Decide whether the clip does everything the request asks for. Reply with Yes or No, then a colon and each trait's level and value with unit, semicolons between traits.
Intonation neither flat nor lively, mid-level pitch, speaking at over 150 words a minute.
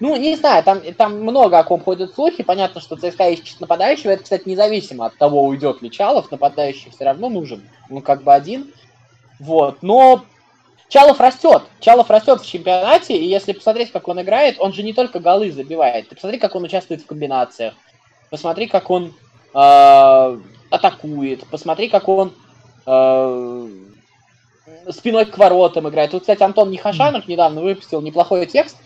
No: wide, 7.2 semitones; medium, 175 Hz; fast, 160 wpm